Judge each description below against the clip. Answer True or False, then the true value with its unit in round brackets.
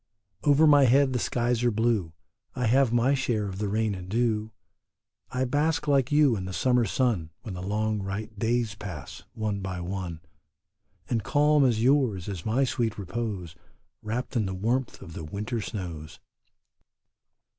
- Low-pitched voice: True (110 Hz)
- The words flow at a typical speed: True (165 wpm)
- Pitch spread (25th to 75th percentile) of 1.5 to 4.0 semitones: False (4.4 semitones)